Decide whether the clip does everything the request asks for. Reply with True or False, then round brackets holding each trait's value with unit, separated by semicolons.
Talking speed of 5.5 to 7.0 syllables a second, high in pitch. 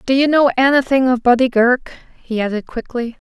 True (5.7 syllables/s; 250 Hz)